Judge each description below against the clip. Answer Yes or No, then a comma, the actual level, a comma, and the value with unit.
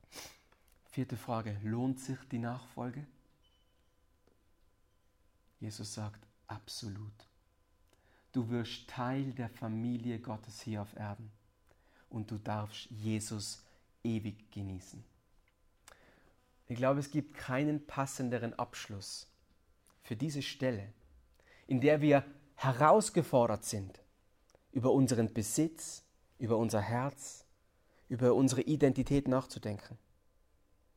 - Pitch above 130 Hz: No, low, 115 Hz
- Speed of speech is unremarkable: No, slow, 95 wpm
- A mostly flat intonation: No, average, 4.3 semitones